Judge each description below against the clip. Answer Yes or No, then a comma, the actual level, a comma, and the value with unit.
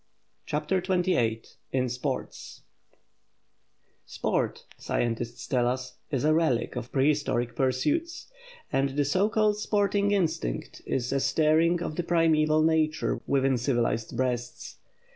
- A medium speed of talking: No, slow, 120 wpm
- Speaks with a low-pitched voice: No, medium, 145 Hz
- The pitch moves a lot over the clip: No, average, 5.0 semitones